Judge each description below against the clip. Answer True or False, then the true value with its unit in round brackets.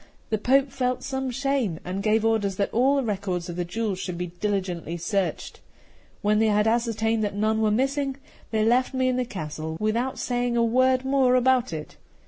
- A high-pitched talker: True (225 Hz)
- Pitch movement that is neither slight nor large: True (4.3 semitones)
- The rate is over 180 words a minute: True (195 wpm)